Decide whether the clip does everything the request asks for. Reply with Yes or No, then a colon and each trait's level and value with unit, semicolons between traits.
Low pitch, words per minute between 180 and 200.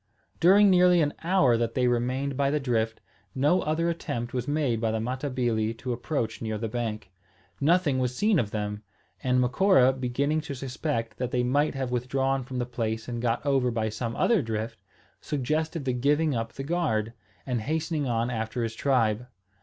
Yes: low, 125 Hz; average, 185 wpm